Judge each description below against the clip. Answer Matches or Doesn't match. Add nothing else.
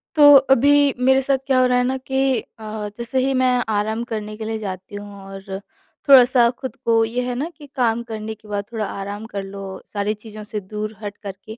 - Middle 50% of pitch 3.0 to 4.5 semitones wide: Matches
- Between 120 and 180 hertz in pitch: Doesn't match